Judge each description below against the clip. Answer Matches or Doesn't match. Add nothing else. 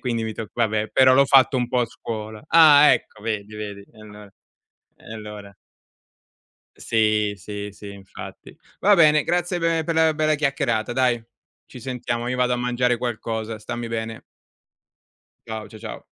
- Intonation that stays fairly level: Doesn't match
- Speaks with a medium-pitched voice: Doesn't match